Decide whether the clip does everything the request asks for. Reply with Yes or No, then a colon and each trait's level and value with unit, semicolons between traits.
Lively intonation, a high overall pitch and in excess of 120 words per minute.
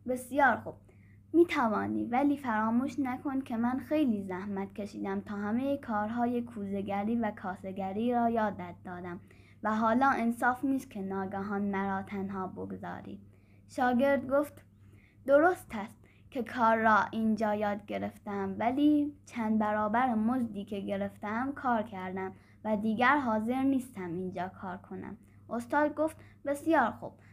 No: average, 4.6 semitones; high, 220 Hz; average, 130 wpm